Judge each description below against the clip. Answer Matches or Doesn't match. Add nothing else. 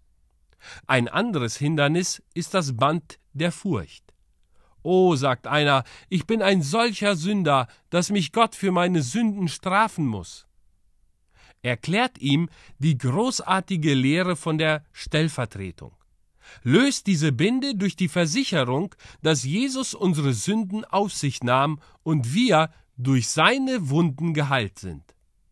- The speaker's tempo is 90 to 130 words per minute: Matches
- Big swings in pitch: Matches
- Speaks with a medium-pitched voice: Matches